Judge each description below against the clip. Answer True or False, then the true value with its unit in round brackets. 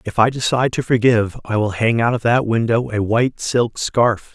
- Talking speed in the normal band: False (220 wpm)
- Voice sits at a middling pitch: False (115 Hz)